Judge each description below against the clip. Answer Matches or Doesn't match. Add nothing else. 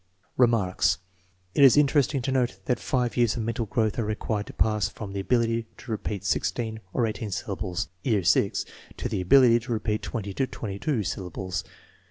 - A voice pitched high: Doesn't match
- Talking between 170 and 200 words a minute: Matches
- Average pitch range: Matches